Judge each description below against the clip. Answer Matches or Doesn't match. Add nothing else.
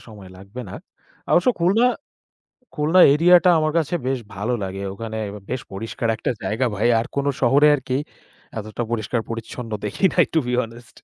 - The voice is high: Doesn't match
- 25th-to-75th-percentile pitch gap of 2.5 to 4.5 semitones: Doesn't match